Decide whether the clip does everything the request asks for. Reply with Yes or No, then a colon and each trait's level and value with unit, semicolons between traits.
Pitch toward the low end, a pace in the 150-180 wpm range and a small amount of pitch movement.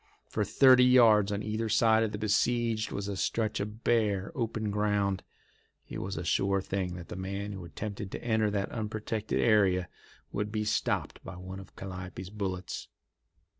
Yes: low, 105 Hz; average, 170 wpm; narrow, 2.2 semitones